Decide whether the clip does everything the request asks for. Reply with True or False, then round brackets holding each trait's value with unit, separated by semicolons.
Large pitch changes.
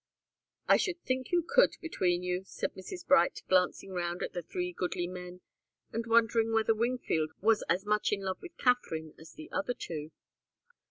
True (5.7 semitones)